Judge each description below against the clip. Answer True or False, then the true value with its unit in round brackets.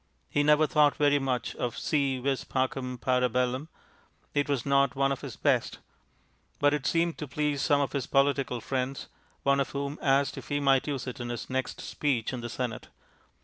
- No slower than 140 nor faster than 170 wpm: False (195 wpm)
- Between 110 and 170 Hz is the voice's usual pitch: True (135 Hz)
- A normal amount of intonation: False (2.2 semitones)